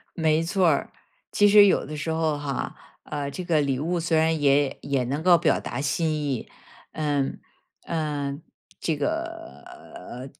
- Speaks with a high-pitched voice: No, medium, 155 Hz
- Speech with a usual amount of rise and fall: Yes, average, 3.2 semitones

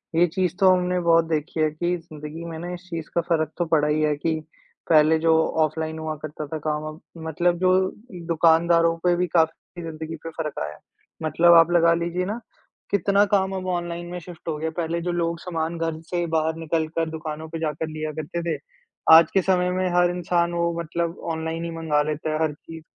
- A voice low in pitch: No, medium, 165 Hz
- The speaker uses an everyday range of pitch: No, narrow, 1.6 semitones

